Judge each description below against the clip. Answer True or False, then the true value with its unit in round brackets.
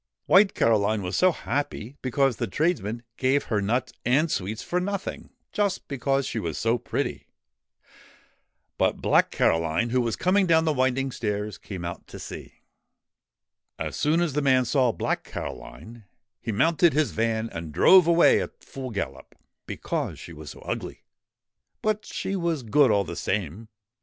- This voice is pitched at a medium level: False (125 Hz)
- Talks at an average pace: True (160 wpm)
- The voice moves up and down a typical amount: False (6.7 semitones)